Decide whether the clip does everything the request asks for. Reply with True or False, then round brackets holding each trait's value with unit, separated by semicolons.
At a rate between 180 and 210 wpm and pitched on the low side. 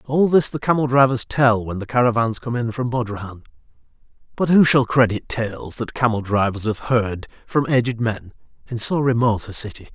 True (185 wpm; 120 Hz)